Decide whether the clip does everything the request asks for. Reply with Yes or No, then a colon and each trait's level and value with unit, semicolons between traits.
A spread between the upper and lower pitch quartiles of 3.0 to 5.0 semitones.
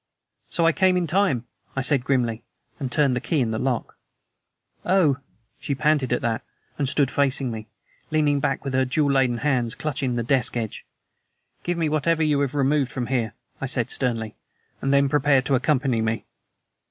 Yes: average, 3.3 semitones